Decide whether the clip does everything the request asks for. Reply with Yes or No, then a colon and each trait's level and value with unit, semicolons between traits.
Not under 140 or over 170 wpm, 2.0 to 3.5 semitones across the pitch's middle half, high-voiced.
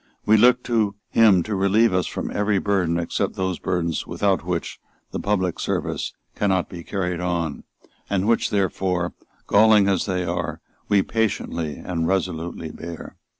No: average, 150 wpm; average, 2.9 semitones; very low, 95 Hz